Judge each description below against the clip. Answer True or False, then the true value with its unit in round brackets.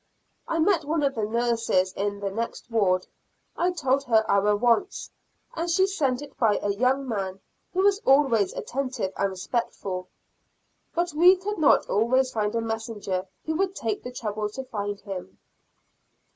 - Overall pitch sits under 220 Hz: False (235 Hz)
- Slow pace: False (165 wpm)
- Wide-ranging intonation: True (6.2 semitones)